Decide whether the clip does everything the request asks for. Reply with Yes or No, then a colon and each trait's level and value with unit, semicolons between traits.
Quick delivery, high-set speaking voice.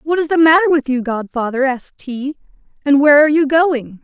Yes: fast, 210 wpm; very high, 285 Hz